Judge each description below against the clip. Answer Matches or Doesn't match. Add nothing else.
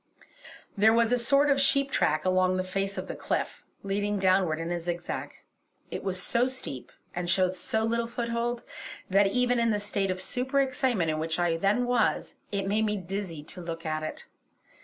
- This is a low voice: Doesn't match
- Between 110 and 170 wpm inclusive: Doesn't match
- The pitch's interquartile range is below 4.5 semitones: Doesn't match